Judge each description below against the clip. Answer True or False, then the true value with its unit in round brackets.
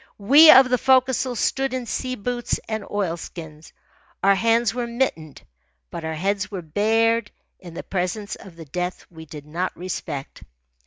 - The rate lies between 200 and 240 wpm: False (160 wpm)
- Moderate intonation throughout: False (6.2 semitones)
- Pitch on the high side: True (200 Hz)